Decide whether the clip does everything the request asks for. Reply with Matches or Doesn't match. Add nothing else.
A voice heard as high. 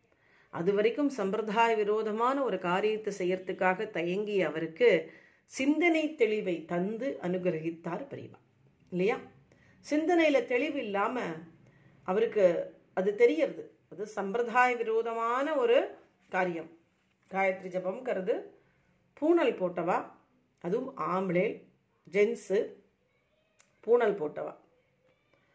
Matches